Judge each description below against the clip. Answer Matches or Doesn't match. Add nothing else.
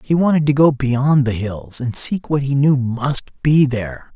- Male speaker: Matches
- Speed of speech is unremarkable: Doesn't match